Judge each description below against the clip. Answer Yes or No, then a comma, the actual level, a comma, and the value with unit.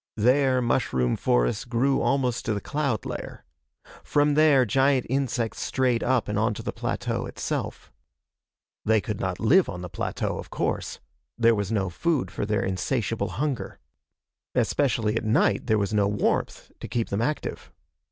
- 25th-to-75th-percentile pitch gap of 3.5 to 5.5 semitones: Yes, average, 4.3 semitones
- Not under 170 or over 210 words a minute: No, average, 160 wpm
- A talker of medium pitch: No, low, 115 Hz